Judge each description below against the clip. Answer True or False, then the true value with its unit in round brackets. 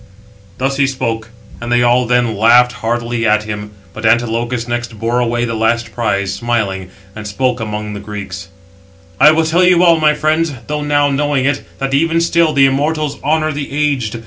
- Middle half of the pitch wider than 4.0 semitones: True (4.5 semitones)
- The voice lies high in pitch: False (120 Hz)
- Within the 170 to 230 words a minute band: True (185 wpm)